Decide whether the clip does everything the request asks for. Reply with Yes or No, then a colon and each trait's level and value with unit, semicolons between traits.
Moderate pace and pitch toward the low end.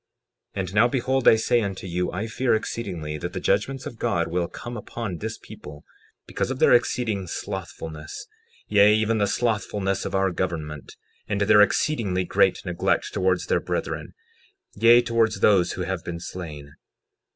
Yes: average, 165 wpm; low, 100 Hz